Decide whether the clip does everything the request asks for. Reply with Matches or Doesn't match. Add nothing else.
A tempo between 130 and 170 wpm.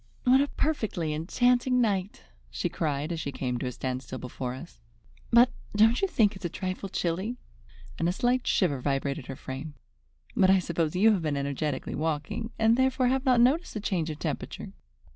Doesn't match